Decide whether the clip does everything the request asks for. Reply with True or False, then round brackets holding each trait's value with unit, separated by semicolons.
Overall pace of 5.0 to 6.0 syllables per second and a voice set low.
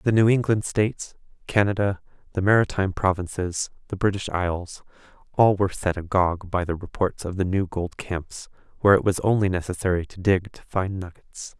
True (5.4 syllables/s; 95 Hz)